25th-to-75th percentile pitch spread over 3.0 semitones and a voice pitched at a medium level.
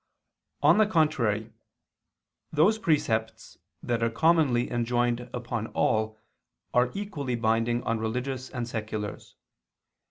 No: average, 4.0 semitones; low, 120 Hz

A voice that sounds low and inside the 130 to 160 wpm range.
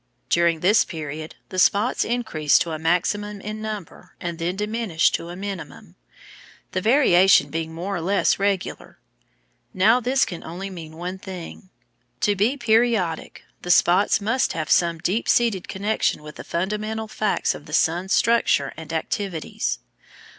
No: high, 190 Hz; average, 155 wpm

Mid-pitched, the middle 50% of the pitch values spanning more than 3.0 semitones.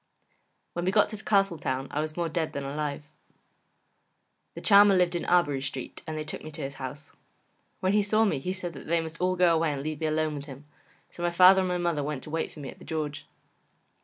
Yes: medium, 160 Hz; average, 3.6 semitones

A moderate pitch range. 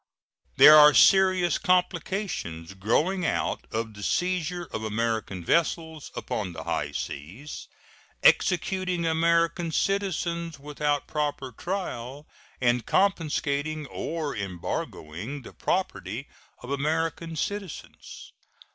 No: wide, 6.5 semitones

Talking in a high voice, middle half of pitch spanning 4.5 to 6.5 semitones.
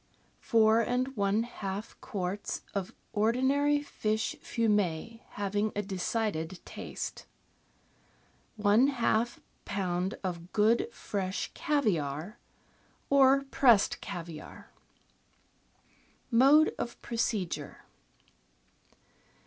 No: high, 215 Hz; average, 3.8 semitones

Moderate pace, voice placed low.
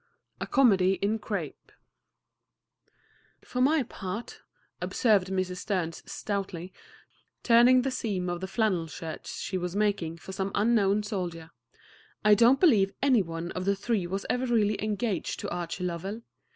No: average, 145 wpm; high, 200 Hz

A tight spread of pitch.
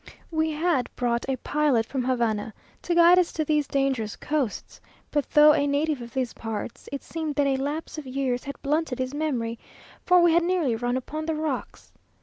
No: average, 3.9 semitones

